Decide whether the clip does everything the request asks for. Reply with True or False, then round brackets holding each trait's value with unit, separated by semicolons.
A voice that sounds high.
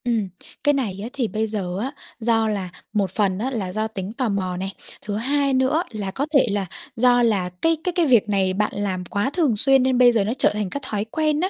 True (220 Hz)